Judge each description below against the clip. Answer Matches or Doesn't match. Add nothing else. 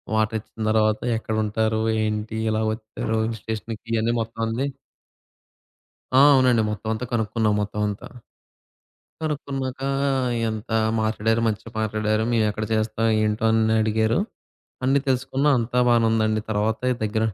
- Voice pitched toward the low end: Matches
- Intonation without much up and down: Matches